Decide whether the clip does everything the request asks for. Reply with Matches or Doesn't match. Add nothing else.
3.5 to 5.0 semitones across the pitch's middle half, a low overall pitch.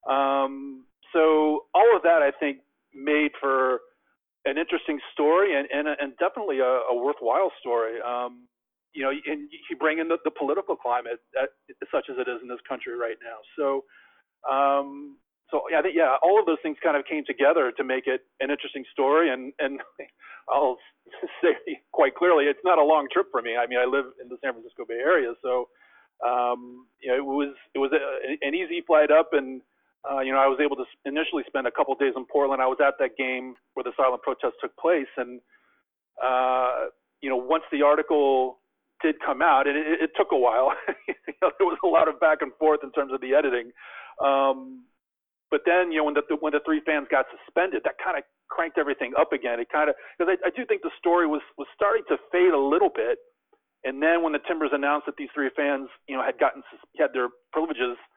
Doesn't match